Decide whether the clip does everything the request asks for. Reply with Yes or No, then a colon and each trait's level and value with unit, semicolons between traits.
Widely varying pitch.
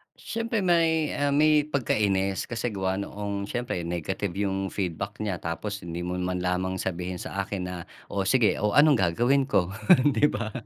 Yes: wide, 6.3 semitones